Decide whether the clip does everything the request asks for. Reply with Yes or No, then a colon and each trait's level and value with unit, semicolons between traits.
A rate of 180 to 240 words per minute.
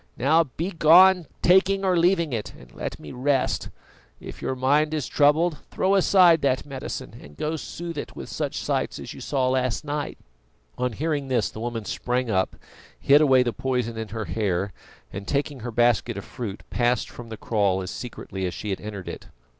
Yes: average, 190 wpm